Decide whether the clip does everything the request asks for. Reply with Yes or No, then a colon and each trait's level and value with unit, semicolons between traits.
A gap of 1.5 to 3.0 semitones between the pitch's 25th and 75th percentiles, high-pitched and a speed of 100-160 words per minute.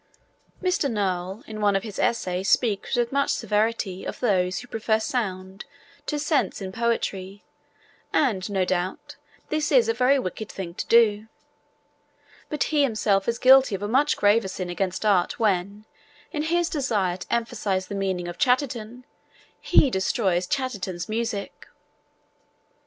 No: average, 4.5 semitones; high, 215 Hz; average, 150 wpm